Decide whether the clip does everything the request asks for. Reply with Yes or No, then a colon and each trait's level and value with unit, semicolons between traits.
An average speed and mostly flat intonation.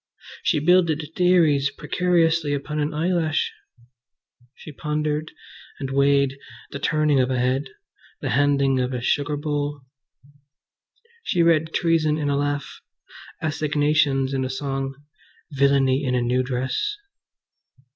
No: slow, 125 wpm; narrow, 2.3 semitones